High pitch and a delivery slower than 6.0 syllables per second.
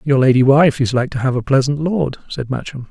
No: low, 135 Hz; 5.5 syllables/s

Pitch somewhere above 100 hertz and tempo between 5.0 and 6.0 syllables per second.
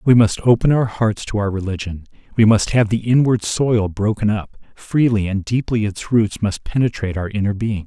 Yes: low, 110 Hz; 5.1 syllables/s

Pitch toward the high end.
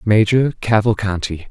No: low, 105 Hz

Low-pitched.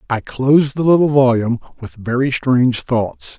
Yes: low, 130 Hz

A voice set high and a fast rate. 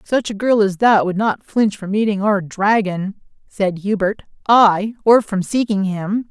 No: high, 205 Hz; average, 180 wpm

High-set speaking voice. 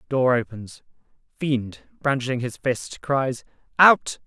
No: low, 130 Hz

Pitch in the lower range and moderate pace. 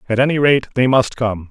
No: low, 120 Hz; fast, 240 wpm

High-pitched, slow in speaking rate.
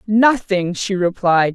Yes: high, 195 Hz; slow, 115 wpm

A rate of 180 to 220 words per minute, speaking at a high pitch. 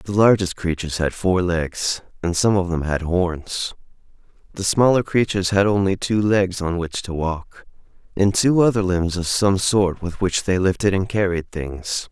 No: average, 185 wpm; very low, 95 Hz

